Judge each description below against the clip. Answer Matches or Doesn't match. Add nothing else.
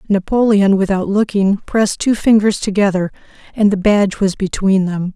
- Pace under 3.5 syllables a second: Doesn't match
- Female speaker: Matches